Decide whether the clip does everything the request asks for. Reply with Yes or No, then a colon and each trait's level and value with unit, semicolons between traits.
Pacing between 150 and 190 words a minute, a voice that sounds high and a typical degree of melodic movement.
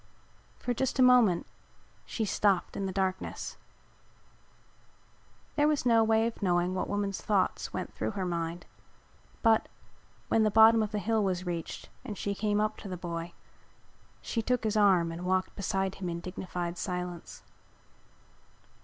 Yes: average, 155 wpm; high, 195 Hz; average, 3.6 semitones